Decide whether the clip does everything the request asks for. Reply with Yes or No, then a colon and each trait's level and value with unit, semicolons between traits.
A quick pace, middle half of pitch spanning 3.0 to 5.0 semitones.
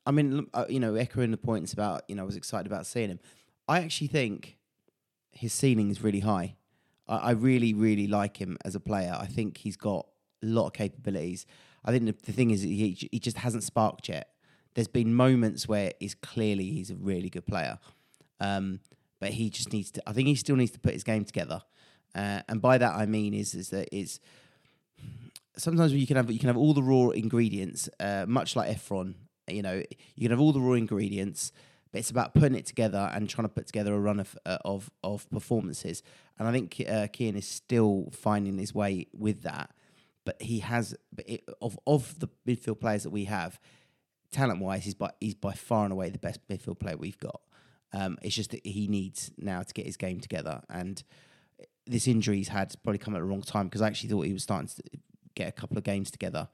Yes: fast, 220 wpm; average, 3.6 semitones